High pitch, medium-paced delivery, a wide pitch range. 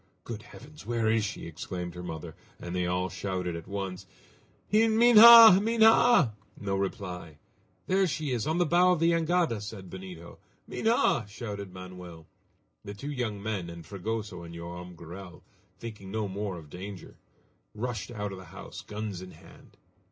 No: low, 100 Hz; average, 160 wpm; wide, 5.7 semitones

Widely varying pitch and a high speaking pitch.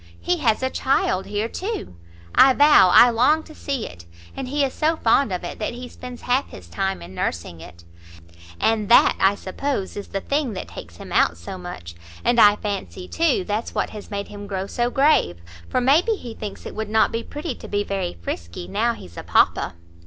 Yes: wide, 5.9 semitones; high, 220 Hz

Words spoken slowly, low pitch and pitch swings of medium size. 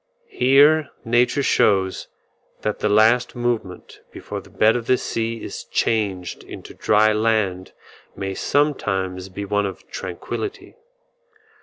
Yes: slow, 125 wpm; low, 110 Hz; average, 4.0 semitones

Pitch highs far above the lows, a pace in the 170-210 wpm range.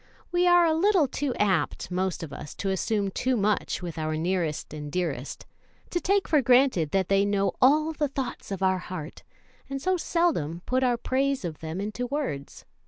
Yes: wide, 8.1 semitones; average, 190 wpm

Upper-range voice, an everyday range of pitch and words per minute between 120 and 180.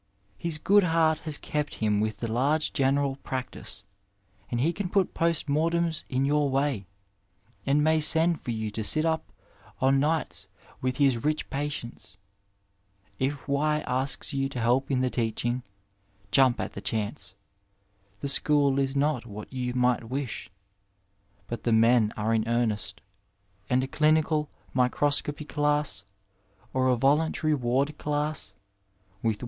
No: low, 135 Hz; average, 4.0 semitones; average, 150 wpm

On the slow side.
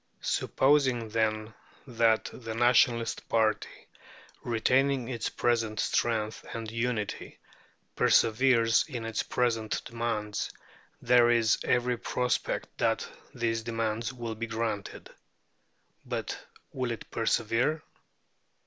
Yes: slow, 100 wpm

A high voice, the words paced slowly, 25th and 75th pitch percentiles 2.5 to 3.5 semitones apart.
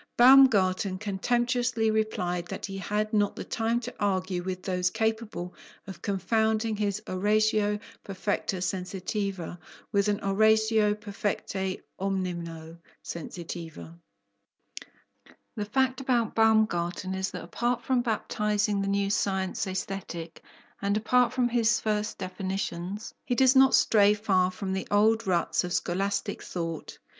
Yes: high, 200 Hz; slow, 125 wpm; average, 2.8 semitones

